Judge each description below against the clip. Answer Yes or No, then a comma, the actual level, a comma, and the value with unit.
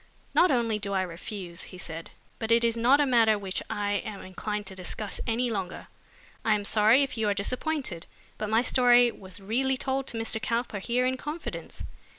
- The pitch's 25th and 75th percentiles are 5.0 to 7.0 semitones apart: No, average, 3.7 semitones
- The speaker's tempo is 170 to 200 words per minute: Yes, average, 195 wpm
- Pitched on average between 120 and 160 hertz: No, high, 220 Hz